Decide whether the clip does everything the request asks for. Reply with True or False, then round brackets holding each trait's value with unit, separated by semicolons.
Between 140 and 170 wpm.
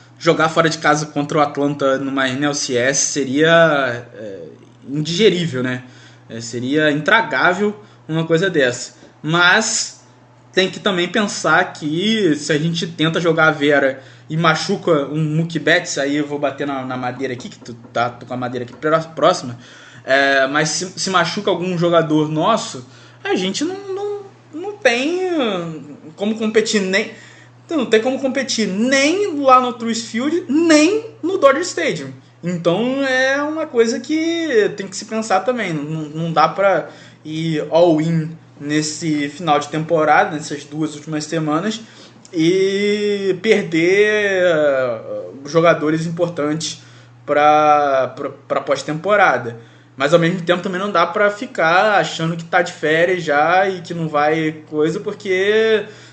True (145 wpm)